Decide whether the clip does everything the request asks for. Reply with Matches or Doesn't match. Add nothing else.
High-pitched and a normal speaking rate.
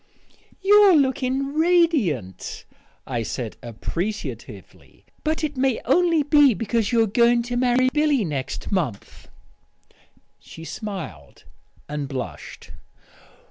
Doesn't match